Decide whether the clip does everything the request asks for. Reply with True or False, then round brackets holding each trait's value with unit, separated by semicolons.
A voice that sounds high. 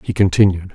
False (95 Hz)